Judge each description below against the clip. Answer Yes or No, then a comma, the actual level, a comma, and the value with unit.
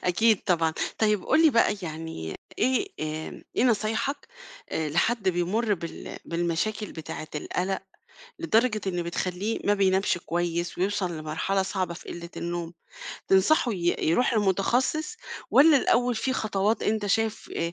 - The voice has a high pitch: Yes, high, 195 Hz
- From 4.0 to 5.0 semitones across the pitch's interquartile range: Yes, average, 4.6 semitones